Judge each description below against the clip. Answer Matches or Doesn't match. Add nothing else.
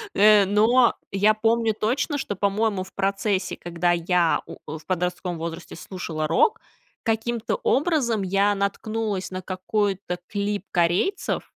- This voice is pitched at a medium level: Doesn't match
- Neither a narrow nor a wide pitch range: Matches